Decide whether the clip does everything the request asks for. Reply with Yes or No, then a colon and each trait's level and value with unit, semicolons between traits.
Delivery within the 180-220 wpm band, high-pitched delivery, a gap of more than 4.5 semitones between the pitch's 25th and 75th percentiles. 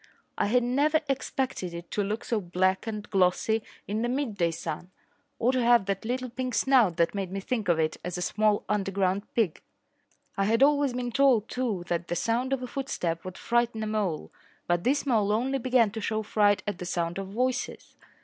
Yes: fast, 205 wpm; high, 215 Hz; average, 4.9 semitones